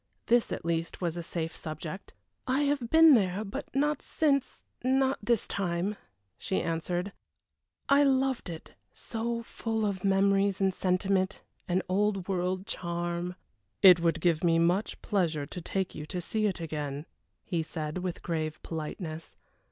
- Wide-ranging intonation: No, average, 4.2 semitones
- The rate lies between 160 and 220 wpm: No, average, 150 wpm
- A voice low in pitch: No, medium, 185 Hz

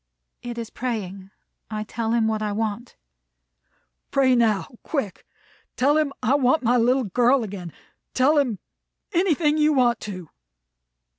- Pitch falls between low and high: No, high, 240 Hz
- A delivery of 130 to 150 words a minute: Yes, average, 140 wpm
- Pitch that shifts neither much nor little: Yes, average, 4.1 semitones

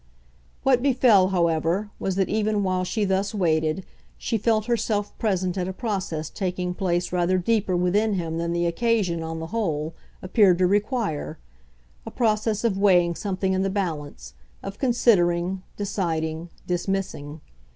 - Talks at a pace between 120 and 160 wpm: Yes, average, 150 wpm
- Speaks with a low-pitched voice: No, high, 190 Hz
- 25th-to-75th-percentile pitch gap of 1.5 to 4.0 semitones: Yes, average, 3.4 semitones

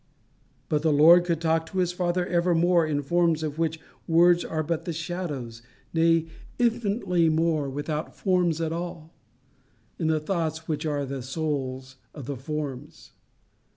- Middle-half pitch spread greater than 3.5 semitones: No, narrow, 2.5 semitones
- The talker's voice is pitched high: No, medium, 160 Hz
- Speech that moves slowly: No, average, 155 wpm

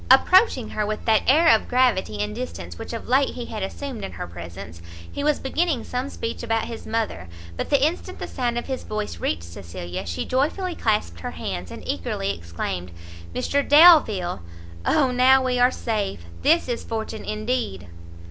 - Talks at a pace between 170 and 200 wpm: Yes, average, 180 wpm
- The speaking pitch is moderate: No, high, 225 Hz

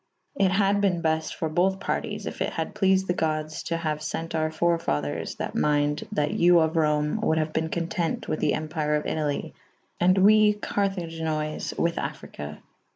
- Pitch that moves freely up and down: No, average, 3.1 semitones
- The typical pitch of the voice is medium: Yes, medium, 160 Hz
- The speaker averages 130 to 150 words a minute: No, average, 185 wpm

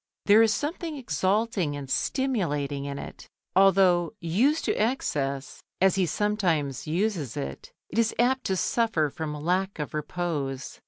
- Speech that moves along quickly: No, average, 145 wpm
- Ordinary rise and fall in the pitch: No, wide, 6.8 semitones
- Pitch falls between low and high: Yes, medium, 180 Hz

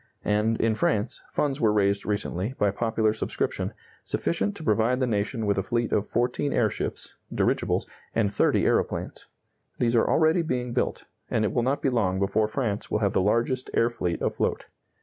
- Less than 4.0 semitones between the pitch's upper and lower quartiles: Yes, average, 3.3 semitones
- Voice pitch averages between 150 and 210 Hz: No, low, 110 Hz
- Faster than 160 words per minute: Yes, average, 180 wpm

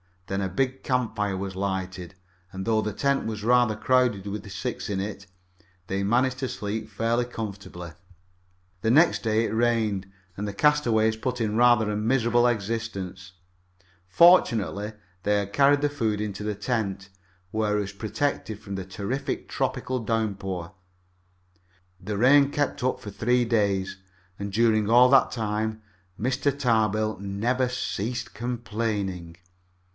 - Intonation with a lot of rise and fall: No, average, 3.5 semitones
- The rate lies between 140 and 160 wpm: Yes, average, 145 wpm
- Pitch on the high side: No, low, 110 Hz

